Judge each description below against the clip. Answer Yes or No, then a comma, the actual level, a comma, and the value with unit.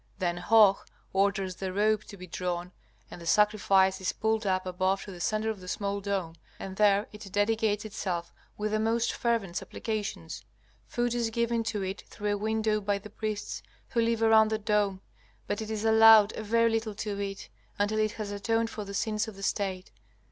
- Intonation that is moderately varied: No, narrow, 2.2 semitones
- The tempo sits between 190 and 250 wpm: Yes, average, 200 wpm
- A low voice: No, high, 210 Hz